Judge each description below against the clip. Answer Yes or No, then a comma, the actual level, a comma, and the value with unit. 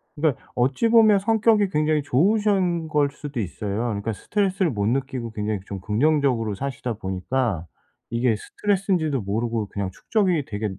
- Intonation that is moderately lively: No, wide, 8.7 semitones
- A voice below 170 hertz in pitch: Yes, low, 135 Hz